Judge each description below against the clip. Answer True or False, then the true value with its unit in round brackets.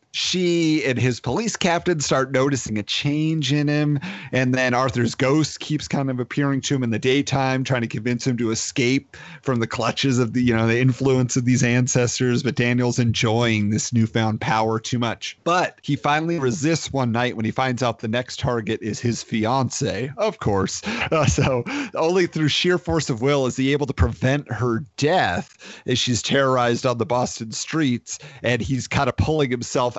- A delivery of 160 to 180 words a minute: False (190 wpm)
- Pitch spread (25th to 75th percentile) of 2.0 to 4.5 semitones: True (3.3 semitones)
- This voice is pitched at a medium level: False (130 Hz)